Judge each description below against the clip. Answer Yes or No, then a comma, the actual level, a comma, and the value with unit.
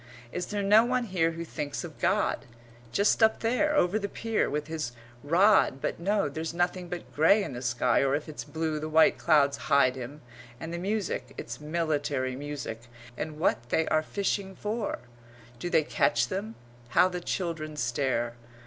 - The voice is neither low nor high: Yes, medium, 160 Hz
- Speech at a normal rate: Yes, average, 180 wpm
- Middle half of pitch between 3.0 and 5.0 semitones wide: No, wide, 5.4 semitones